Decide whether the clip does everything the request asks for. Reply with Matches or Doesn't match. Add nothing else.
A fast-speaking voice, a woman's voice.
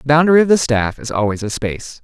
Doesn't match